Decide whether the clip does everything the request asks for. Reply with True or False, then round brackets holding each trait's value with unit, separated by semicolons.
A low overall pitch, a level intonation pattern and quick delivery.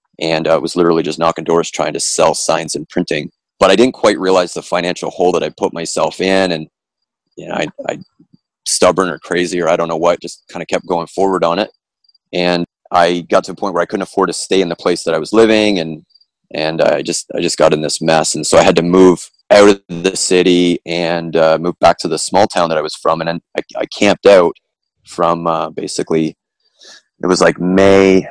True (85 Hz; 2.3 semitones; 235 wpm)